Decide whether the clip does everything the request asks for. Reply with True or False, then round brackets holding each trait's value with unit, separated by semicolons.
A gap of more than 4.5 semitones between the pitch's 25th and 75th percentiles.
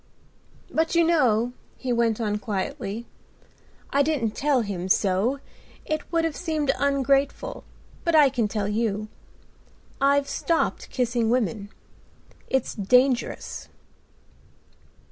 True (4.9 semitones)